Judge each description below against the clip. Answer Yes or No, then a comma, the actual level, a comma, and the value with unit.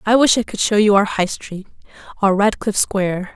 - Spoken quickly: No, average, 195 wpm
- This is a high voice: Yes, high, 205 Hz